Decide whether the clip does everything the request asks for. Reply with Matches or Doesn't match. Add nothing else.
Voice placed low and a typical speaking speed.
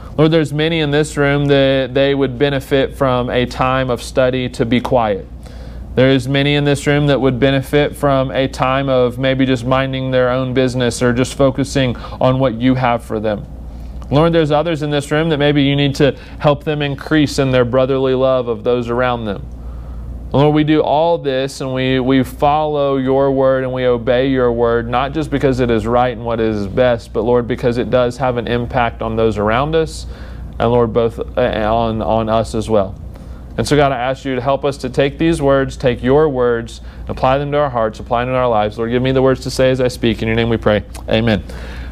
Doesn't match